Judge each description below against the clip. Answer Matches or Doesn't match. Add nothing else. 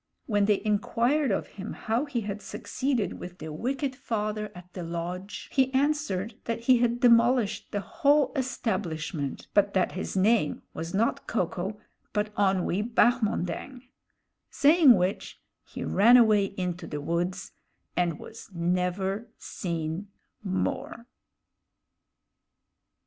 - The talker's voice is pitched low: Doesn't match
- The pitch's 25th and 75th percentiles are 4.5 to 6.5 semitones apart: Matches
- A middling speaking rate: Doesn't match